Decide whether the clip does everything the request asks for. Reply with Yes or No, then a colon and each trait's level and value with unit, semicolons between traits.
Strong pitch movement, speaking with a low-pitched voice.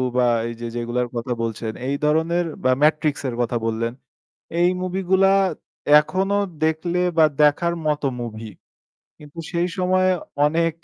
No: wide, 6.4 semitones; medium, 150 Hz